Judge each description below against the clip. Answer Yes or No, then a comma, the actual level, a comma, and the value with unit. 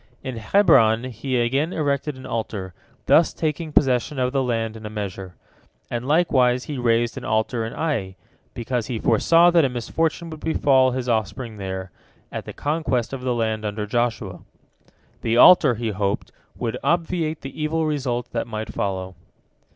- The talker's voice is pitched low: Yes, low, 125 Hz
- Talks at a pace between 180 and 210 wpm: No, average, 165 wpm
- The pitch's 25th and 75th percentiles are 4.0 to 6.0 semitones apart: Yes, average, 4.8 semitones